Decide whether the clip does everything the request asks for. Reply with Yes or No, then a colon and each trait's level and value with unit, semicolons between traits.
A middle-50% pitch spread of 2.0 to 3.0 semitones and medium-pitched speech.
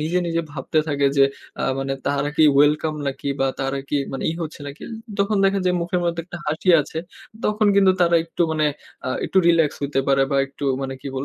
No: average, 3.7 semitones; medium, 155 Hz